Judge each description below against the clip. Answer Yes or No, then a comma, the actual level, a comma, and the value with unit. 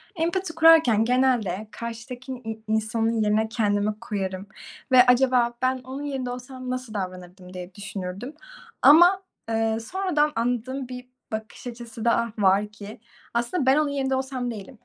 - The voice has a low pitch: No, high, 235 Hz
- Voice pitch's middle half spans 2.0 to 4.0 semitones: Yes, average, 3.4 semitones